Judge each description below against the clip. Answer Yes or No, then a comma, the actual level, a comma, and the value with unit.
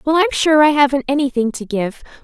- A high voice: Yes, very high, 280 Hz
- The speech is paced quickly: Yes, fast, 215 wpm